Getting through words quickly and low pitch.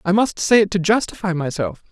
No: fast, 220 wpm; medium, 185 Hz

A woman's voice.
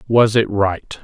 No: male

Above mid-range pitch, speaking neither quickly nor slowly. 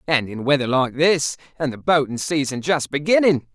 No: medium, 145 Hz; average, 185 wpm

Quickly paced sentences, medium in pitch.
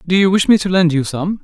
Yes: fast, 335 wpm; medium, 175 Hz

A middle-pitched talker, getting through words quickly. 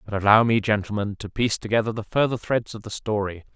No: low, 105 Hz; fast, 220 wpm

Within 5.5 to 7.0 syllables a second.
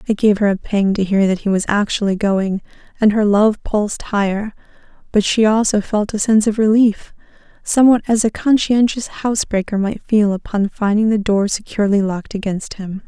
No: 5.3 syllables/s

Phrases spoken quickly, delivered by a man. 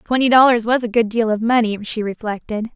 No: fast, 215 wpm; female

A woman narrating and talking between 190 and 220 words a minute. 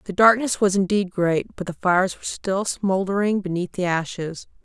No: female; average, 180 wpm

